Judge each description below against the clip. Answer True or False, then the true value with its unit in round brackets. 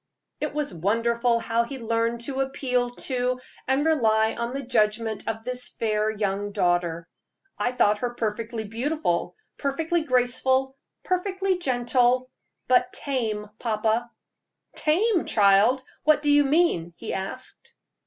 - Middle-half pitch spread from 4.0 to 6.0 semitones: False (3.6 semitones)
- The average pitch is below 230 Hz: False (240 Hz)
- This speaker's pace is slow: True (130 wpm)